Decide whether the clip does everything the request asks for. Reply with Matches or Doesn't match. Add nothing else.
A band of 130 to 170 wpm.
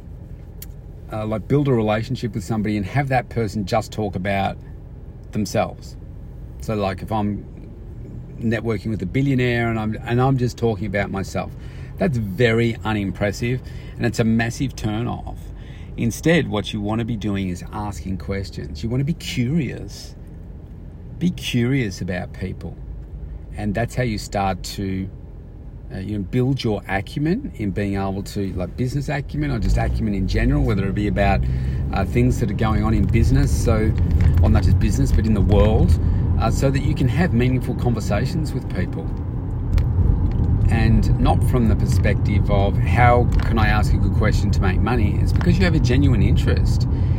Doesn't match